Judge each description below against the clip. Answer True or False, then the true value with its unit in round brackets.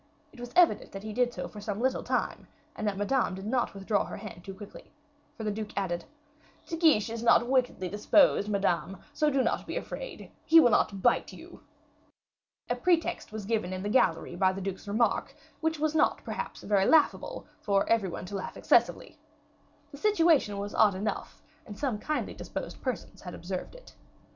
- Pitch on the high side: True (210 Hz)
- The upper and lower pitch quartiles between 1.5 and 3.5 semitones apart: False (5.2 semitones)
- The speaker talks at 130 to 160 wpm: False (190 wpm)